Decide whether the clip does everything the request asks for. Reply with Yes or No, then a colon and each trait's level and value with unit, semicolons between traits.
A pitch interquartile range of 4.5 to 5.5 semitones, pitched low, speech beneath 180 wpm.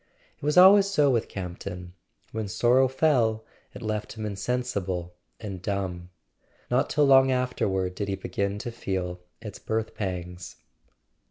Yes: average, 5.1 semitones; low, 105 Hz; average, 145 wpm